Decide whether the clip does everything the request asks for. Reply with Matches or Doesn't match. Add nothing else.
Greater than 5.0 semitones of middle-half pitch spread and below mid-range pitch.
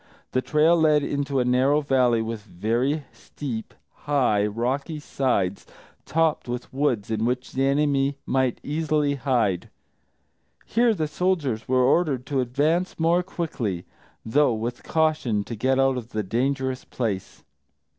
Doesn't match